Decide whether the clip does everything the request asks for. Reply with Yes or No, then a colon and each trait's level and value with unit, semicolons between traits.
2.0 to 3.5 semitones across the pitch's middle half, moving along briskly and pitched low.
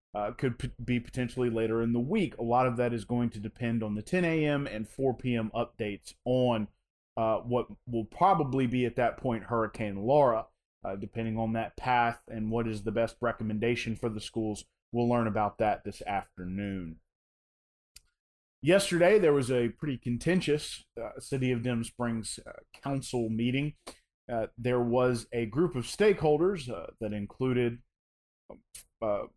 No: narrow, 2.4 semitones; average, 165 wpm; low, 120 Hz